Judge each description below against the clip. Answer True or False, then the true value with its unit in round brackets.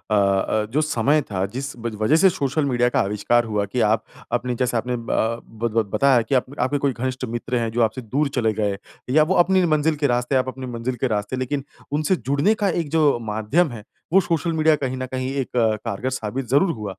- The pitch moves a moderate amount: True (4.1 semitones)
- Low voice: True (125 Hz)